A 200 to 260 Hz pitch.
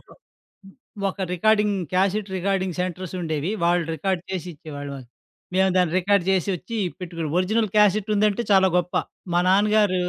No: medium, 185 Hz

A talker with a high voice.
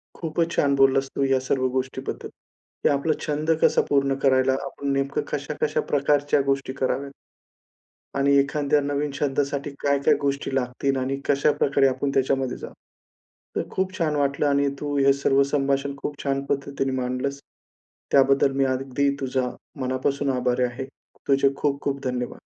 No: medium, 140 Hz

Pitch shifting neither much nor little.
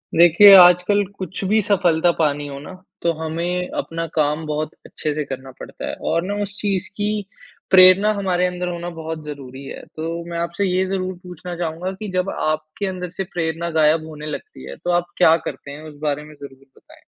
Yes: average, 3.1 semitones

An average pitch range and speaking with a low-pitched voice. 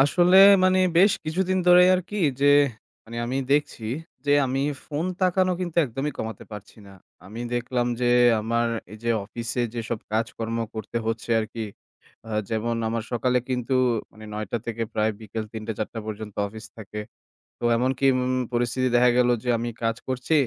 Yes: average, 3.5 semitones; low, 120 Hz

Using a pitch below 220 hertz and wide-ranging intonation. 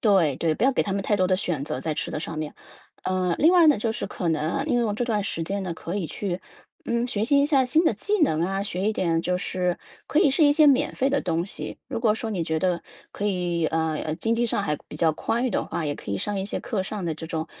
Yes: high, 195 Hz; wide, 6.0 semitones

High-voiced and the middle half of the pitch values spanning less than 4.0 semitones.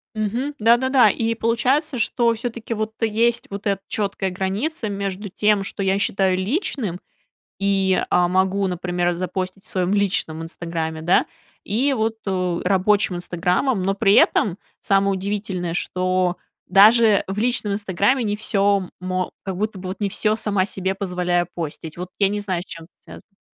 Yes: high, 195 Hz; average, 2.9 semitones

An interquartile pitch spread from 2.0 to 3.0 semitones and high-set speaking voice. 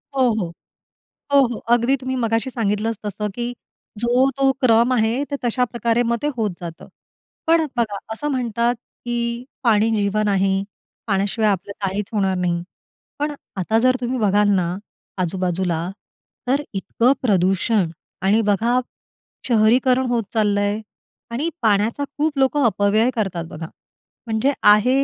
No: average, 3.7 semitones; high, 225 Hz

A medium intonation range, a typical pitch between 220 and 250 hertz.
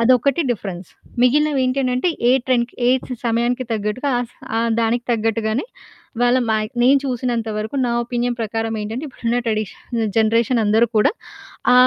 No: narrow, 2.2 semitones; high, 235 Hz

